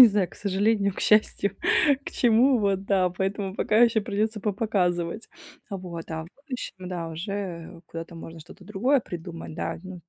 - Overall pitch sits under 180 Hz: No, high, 195 Hz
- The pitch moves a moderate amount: Yes, average, 3.6 semitones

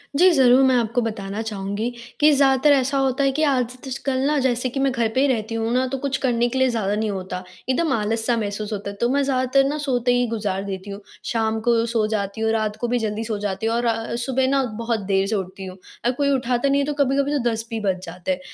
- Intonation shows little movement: No, average, 3.8 semitones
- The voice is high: Yes, high, 235 Hz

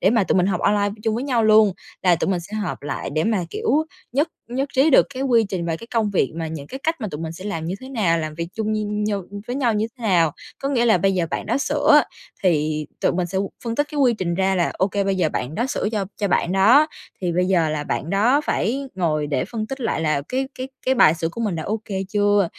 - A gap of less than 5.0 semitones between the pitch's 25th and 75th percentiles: No, average, 5.3 semitones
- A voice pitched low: No, high, 200 Hz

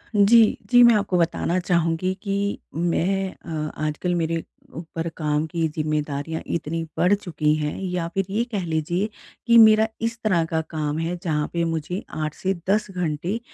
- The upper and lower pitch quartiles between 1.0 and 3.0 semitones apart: No, average, 3.7 semitones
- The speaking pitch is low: No, medium, 170 Hz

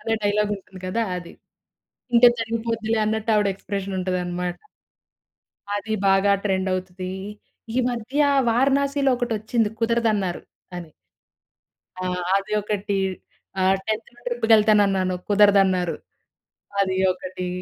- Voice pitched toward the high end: Yes, high, 205 Hz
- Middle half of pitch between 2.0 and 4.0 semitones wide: Yes, average, 3.2 semitones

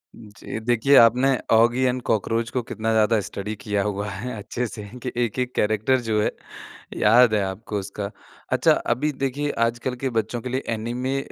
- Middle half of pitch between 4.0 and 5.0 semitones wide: No, average, 2.9 semitones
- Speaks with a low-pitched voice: Yes, low, 115 Hz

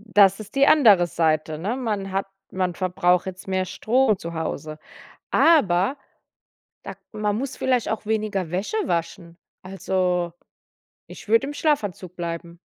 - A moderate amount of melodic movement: Yes, average, 3.9 semitones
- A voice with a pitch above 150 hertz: Yes, high, 190 Hz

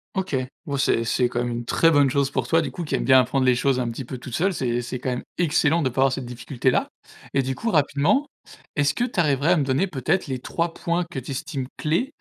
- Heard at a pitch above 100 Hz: Yes, low, 135 Hz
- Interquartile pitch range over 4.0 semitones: Yes, average, 4.4 semitones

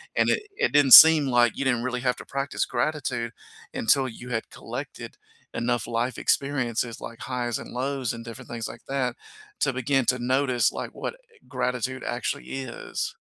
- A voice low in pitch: Yes, low, 125 Hz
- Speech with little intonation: Yes, narrow, 2.2 semitones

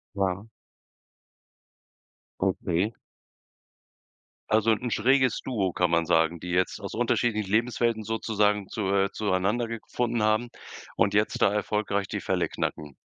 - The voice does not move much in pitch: No, average, 3.0 semitones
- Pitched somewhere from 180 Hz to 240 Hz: No, low, 105 Hz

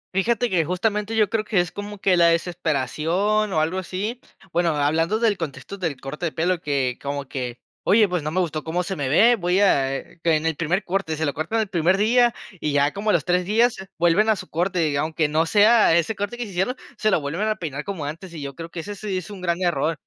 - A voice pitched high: No, medium, 175 Hz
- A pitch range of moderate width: Yes, average, 4.6 semitones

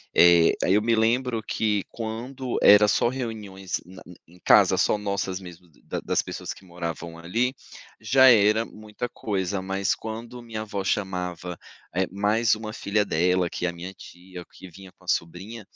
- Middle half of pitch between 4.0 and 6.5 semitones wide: No, average, 3.6 semitones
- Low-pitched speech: Yes, low, 100 Hz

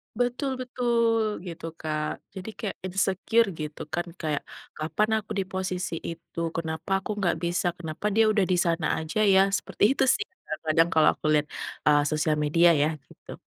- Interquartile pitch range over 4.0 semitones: Yes, average, 4.8 semitones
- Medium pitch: Yes, medium, 175 Hz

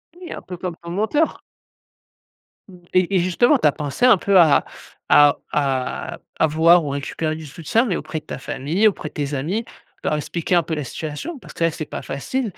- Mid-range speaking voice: Yes, medium, 165 Hz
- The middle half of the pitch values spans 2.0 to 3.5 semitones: No, average, 4.9 semitones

